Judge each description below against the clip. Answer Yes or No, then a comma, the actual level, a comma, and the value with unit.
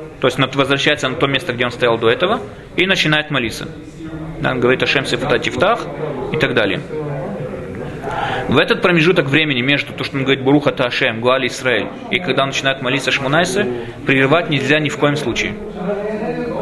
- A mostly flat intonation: No, average, 3.4 semitones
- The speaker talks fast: Yes, fast, 175 wpm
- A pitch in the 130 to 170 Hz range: Yes, medium, 140 Hz